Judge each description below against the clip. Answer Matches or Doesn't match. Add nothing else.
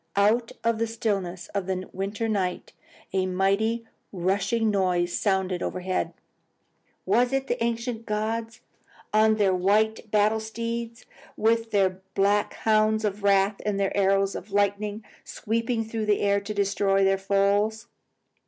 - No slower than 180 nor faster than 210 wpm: Doesn't match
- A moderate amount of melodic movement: Doesn't match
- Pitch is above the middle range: Matches